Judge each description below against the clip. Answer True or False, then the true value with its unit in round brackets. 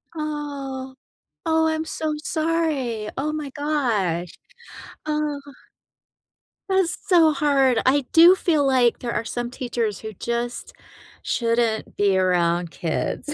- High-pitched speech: True (270 Hz)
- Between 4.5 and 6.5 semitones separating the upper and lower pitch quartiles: True (5.0 semitones)